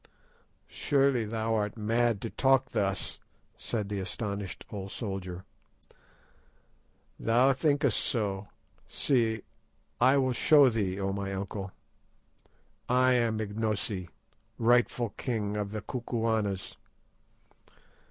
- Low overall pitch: Yes, low, 110 Hz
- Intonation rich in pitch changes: No, average, 3.5 semitones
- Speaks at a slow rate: Yes, slow, 105 wpm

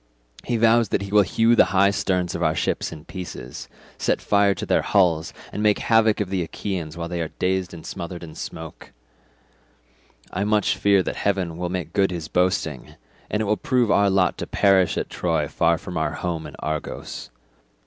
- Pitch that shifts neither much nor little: Yes, average, 3.2 semitones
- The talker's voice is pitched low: Yes, very low, 95 Hz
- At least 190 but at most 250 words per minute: Yes, average, 200 wpm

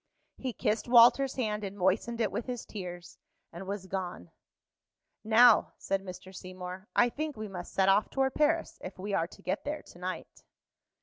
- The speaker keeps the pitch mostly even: No, average, 4.5 semitones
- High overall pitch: Yes, high, 200 Hz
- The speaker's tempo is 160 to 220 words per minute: Yes, average, 180 wpm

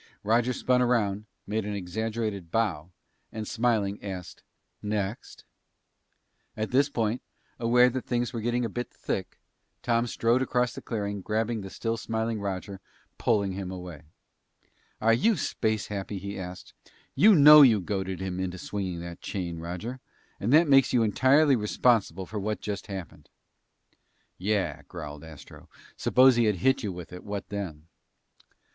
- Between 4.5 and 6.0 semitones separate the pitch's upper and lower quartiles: No, average, 3.9 semitones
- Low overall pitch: Yes, low, 105 Hz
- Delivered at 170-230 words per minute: No, average, 155 wpm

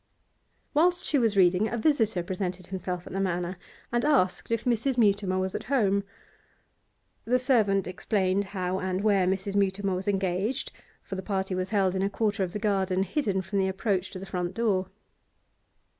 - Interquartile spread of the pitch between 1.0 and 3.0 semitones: Yes, narrow, 2.6 semitones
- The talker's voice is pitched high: Yes, high, 195 Hz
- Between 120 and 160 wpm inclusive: No, average, 180 wpm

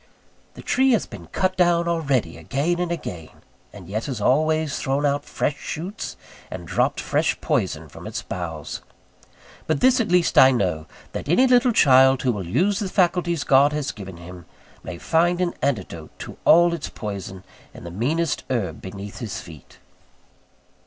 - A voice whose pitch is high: No, medium, 140 Hz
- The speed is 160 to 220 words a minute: Yes, average, 170 wpm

